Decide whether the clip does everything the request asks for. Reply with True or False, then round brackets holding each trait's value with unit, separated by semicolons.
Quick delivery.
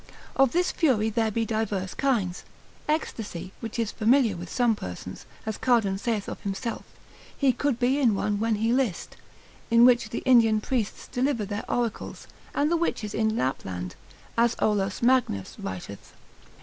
False (160 wpm)